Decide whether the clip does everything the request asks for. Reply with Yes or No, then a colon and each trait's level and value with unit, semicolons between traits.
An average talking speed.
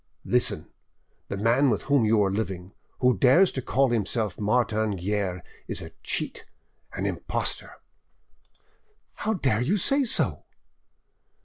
No: slow, 130 wpm